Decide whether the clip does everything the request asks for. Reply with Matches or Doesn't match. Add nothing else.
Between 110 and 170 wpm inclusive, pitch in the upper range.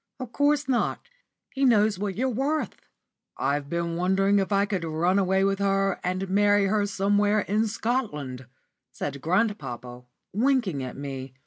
Matches